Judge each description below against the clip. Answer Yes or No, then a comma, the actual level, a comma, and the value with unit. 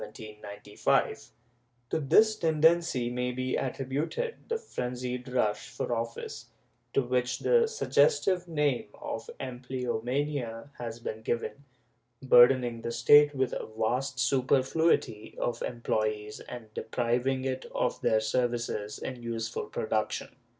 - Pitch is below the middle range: Yes, low, 125 Hz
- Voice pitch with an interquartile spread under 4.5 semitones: Yes, average, 2.9 semitones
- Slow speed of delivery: Yes, slow, 120 wpm